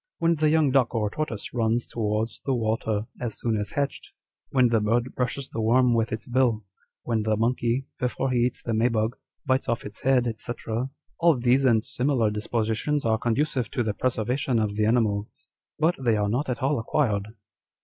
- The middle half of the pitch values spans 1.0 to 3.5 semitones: Yes, average, 2.9 semitones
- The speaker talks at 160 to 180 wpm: No, average, 195 wpm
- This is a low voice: Yes, low, 120 Hz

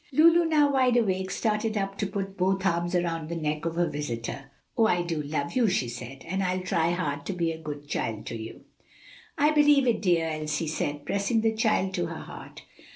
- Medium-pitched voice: Yes, medium, 175 Hz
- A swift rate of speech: Yes, fast, 215 wpm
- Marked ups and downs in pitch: Yes, wide, 5.8 semitones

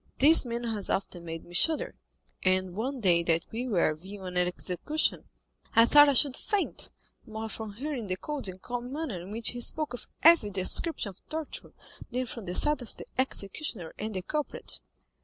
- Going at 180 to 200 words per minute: Yes, average, 190 wpm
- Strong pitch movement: Yes, wide, 6.8 semitones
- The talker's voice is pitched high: Yes, high, 225 Hz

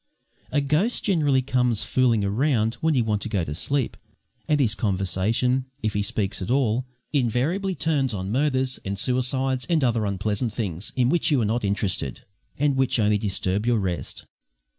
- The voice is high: No, low, 120 Hz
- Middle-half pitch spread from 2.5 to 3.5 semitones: No, average, 4.7 semitones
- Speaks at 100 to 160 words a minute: No, average, 175 wpm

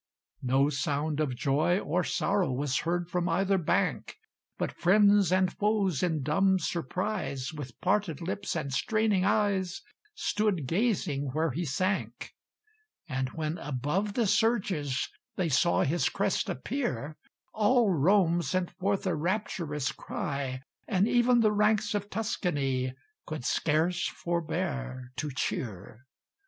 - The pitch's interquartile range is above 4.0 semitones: Yes, wide, 5.6 semitones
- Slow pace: Yes, slow, 130 wpm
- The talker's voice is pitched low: No, medium, 175 Hz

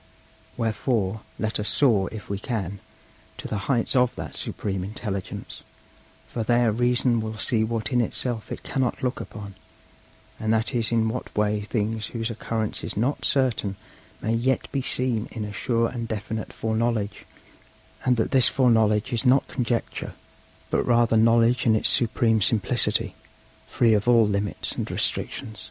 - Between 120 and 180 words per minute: Yes, average, 160 wpm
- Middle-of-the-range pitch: No, low, 115 Hz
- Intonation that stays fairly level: Yes, narrow, 2.2 semitones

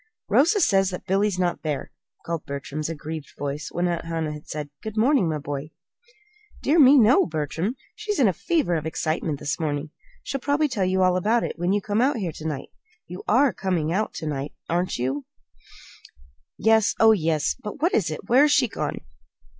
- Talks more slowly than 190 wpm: No, average, 195 wpm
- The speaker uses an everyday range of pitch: No, wide, 6.3 semitones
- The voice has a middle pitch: Yes, medium, 180 Hz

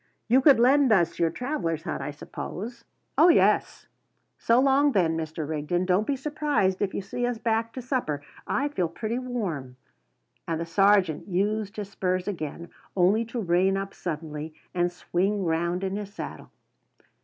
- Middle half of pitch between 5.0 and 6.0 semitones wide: Yes, wide, 5.6 semitones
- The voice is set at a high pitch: Yes, high, 195 Hz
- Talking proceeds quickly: No, average, 165 wpm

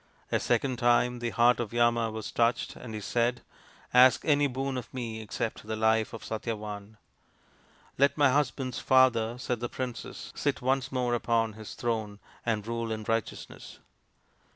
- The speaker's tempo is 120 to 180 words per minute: Yes, average, 170 wpm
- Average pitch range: No, narrow, 2.2 semitones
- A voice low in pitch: Yes, low, 120 Hz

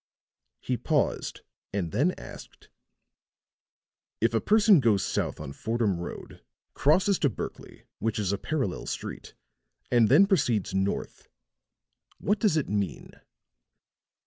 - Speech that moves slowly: Yes, slow, 120 wpm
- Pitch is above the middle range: No, low, 120 Hz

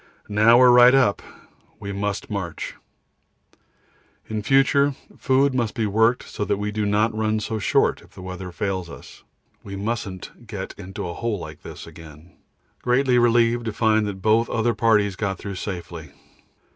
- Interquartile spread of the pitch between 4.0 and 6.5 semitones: No, average, 3.2 semitones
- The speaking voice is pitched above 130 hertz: No, low, 105 Hz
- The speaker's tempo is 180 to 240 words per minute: No, average, 170 wpm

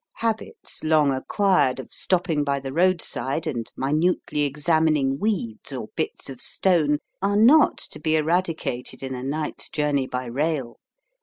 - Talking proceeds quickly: No, average, 145 wpm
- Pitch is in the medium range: Yes, medium, 150 Hz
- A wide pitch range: No, average, 4.3 semitones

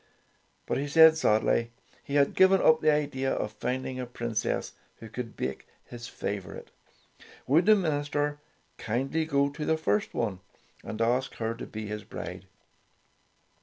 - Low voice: Yes, low, 130 Hz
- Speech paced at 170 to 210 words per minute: No, average, 155 wpm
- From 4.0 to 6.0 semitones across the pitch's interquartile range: Yes, average, 4.8 semitones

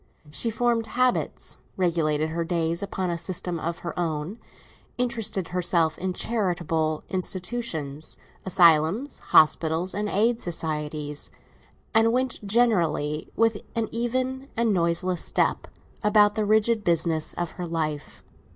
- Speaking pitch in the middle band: Yes, medium, 180 Hz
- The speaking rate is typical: No, slow, 125 wpm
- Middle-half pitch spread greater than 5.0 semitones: Yes, wide, 5.5 semitones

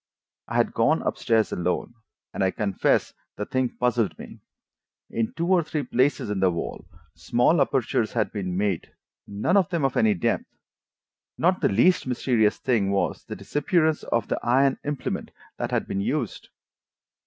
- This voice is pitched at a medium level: No, low, 120 Hz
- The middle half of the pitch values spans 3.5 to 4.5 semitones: No, wide, 5.4 semitones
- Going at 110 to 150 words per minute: No, average, 165 wpm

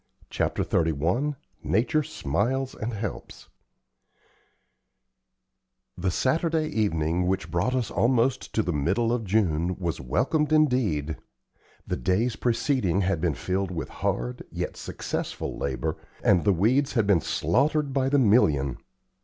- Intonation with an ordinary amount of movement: No, wide, 7.5 semitones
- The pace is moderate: No, slow, 130 wpm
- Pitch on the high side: No, low, 105 Hz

